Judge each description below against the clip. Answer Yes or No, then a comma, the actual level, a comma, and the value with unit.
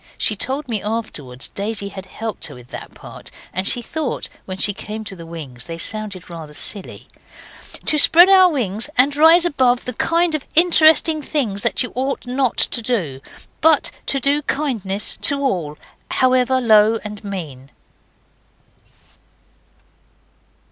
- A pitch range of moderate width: No, wide, 6.7 semitones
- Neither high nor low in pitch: No, high, 225 Hz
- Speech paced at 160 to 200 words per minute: No, average, 150 wpm